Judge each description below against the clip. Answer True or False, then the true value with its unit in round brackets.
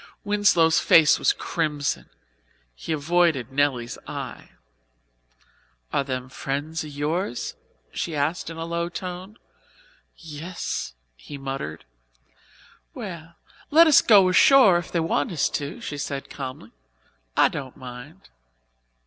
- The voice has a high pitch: False (155 Hz)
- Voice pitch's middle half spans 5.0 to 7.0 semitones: False (4.0 semitones)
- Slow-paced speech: True (125 wpm)